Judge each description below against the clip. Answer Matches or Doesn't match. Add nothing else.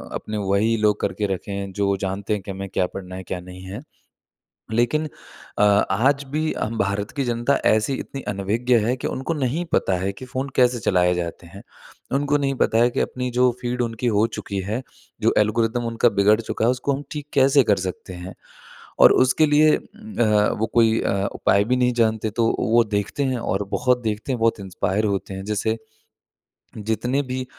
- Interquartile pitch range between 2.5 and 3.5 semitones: Doesn't match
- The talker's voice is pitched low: Matches